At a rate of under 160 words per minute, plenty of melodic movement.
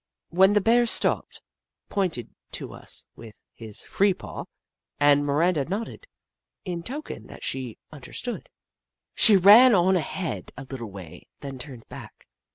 Yes: average, 140 wpm; wide, 7.2 semitones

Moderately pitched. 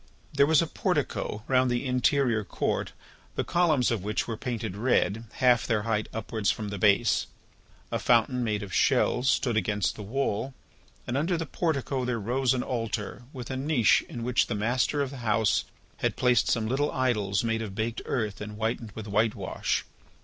No: low, 120 Hz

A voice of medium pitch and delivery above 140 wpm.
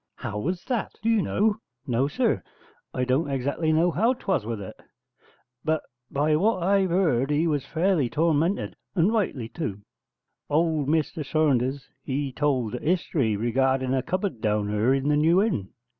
Yes: medium, 150 Hz; average, 165 wpm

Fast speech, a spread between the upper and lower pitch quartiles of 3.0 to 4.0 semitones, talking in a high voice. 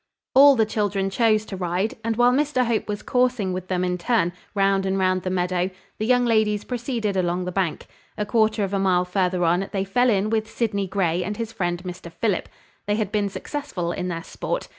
Yes: fast, 215 wpm; average, 3.5 semitones; high, 200 Hz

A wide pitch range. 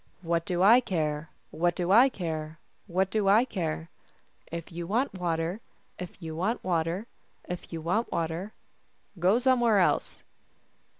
No: average, 3.9 semitones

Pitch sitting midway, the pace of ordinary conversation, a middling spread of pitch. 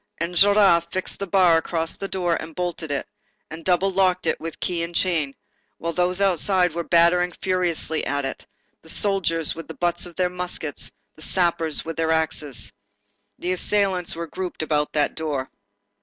No: medium, 170 Hz; average, 170 wpm; narrow, 2.1 semitones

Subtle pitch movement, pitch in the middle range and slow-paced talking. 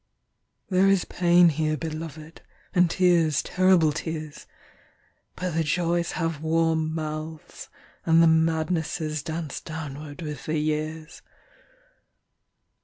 Yes: narrow, 1.5 semitones; medium, 160 Hz; slow, 95 wpm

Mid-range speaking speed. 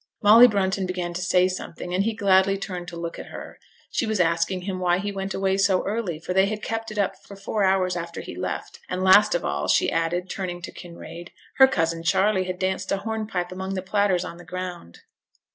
No: fast, 225 wpm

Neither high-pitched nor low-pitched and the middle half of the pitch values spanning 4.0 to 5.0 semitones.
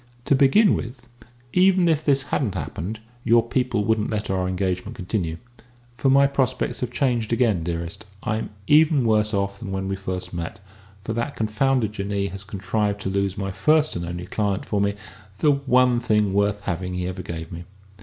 No: low, 105 Hz; average, 4.7 semitones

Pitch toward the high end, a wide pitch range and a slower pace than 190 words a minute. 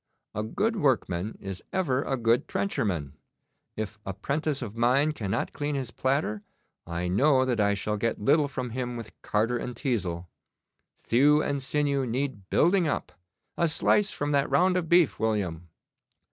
No: low, 125 Hz; wide, 5.7 semitones; average, 160 wpm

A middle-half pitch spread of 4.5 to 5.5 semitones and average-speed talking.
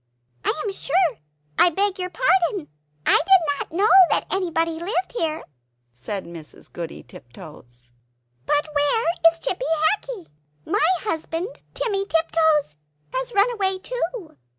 No: average, 4.9 semitones; slow, 130 wpm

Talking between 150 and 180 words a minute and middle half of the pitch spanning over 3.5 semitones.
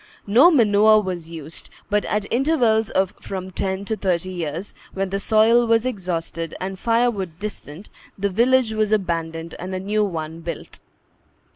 Yes: average, 155 wpm; average, 4.0 semitones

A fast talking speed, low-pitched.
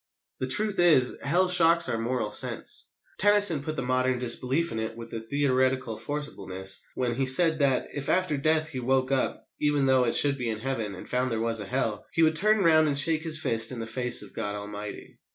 Yes: fast, 220 wpm; low, 130 Hz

